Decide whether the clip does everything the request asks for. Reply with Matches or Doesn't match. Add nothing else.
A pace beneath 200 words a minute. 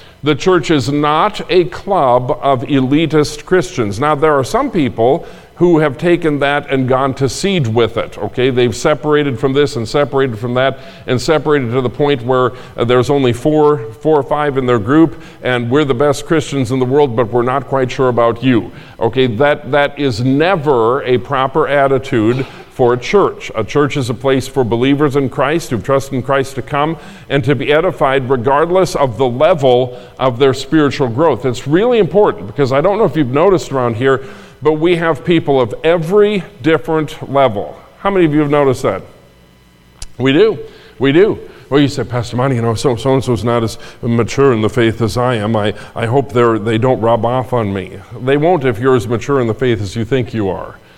Doesn't match